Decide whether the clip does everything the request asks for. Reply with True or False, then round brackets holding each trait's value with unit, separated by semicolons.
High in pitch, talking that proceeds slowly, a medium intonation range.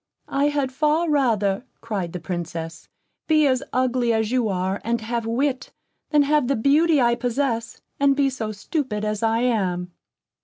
False (240 Hz; 165 wpm; 4.7 semitones)